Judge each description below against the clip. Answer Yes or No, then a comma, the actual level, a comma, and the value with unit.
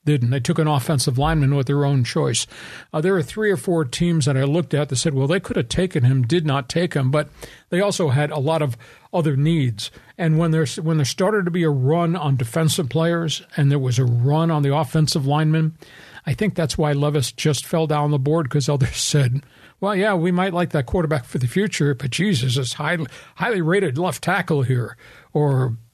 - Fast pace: Yes, fast, 225 wpm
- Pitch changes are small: No, average, 3.5 semitones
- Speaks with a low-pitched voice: No, medium, 155 Hz